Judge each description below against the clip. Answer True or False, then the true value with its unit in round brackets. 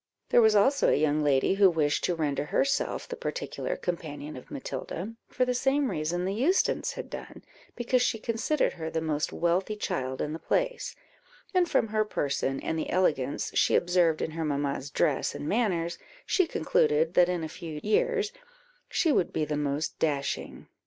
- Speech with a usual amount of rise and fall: False (7.2 semitones)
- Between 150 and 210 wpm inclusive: True (180 wpm)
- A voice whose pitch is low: False (170 Hz)